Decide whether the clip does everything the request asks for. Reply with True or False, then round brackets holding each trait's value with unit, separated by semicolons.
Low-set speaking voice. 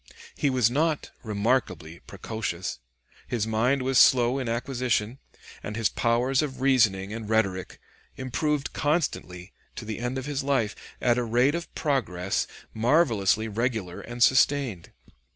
True (120 Hz)